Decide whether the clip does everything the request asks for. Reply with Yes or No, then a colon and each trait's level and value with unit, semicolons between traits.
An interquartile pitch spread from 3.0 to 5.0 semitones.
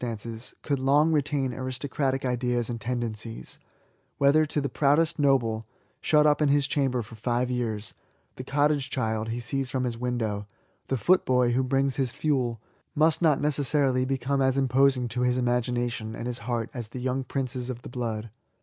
No: narrow, 2.6 semitones